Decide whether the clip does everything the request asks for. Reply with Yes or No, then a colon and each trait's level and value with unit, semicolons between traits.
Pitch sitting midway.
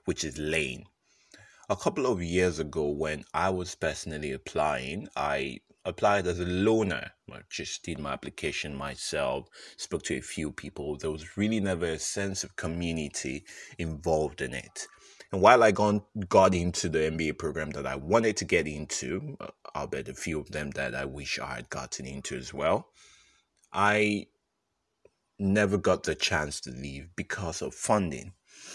No: very low, 85 Hz